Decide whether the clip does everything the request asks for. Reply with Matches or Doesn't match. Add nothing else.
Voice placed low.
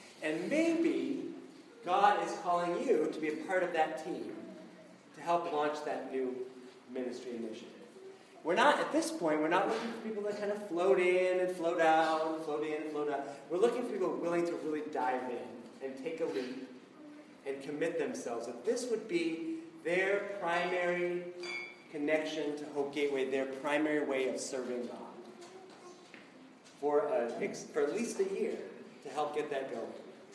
Doesn't match